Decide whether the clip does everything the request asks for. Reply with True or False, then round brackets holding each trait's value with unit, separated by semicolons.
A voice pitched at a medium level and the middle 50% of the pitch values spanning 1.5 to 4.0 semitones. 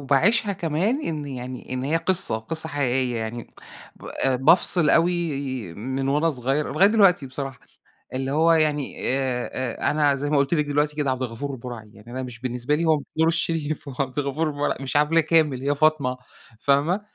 True (145 Hz; 3.6 semitones)